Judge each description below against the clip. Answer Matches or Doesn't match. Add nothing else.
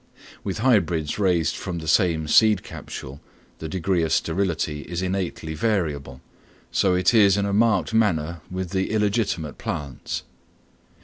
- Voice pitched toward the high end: Doesn't match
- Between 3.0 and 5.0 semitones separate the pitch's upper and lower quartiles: Matches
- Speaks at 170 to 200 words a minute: Doesn't match